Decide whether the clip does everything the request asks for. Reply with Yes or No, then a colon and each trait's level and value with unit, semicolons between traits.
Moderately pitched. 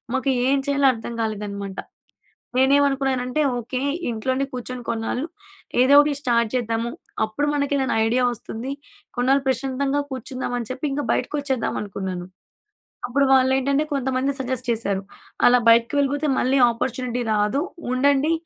No: very high, 255 Hz